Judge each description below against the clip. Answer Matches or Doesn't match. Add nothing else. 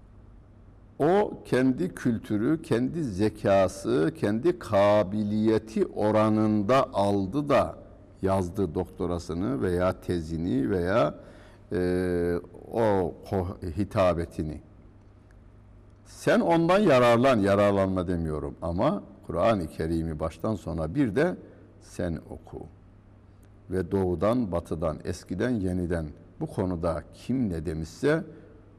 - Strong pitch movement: Doesn't match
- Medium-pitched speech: Doesn't match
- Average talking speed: Doesn't match